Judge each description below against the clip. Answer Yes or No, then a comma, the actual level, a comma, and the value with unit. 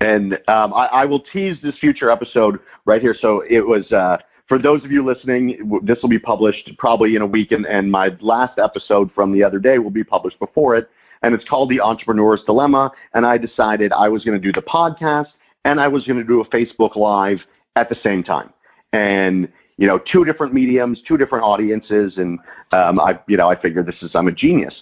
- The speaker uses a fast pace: Yes, fast, 225 wpm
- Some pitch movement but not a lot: Yes, average, 4.1 semitones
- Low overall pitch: Yes, low, 115 Hz